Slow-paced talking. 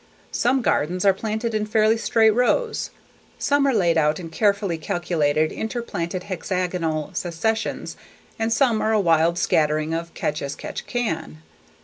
No: average, 145 wpm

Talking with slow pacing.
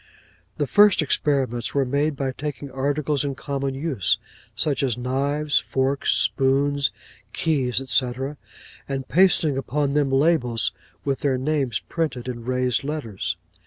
Yes: slow, 130 wpm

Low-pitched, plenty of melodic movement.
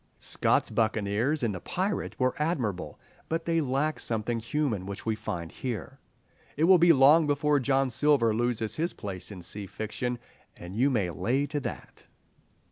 Yes: low, 125 Hz; wide, 5.9 semitones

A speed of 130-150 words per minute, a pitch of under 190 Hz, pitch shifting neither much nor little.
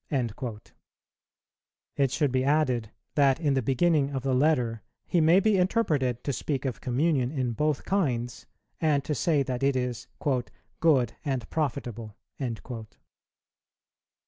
Yes: slow, 135 wpm; low, 135 Hz; average, 3.7 semitones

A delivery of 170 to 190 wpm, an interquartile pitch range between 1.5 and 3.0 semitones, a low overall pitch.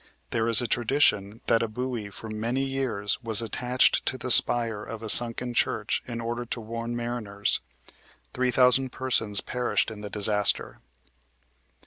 No: average, 155 wpm; narrow, 2.4 semitones; low, 115 Hz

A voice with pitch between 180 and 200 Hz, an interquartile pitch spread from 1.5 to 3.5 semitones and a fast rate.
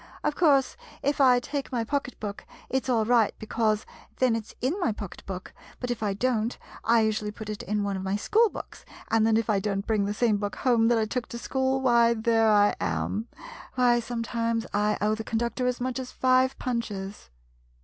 No: high, 230 Hz; average, 3.0 semitones; fast, 220 wpm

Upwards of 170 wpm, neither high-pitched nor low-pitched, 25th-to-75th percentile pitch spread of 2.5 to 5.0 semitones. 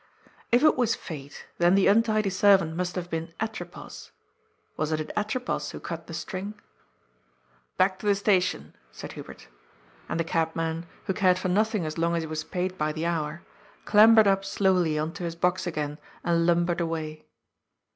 Yes: average, 180 wpm; medium, 175 Hz; average, 3.5 semitones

